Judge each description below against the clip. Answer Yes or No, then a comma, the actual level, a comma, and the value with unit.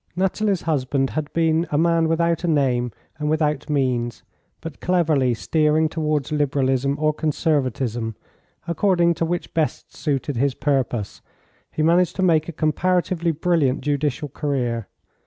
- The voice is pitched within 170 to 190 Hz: No, medium, 150 Hz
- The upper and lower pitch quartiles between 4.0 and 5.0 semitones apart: No, average, 3.6 semitones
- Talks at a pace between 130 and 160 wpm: Yes, average, 140 wpm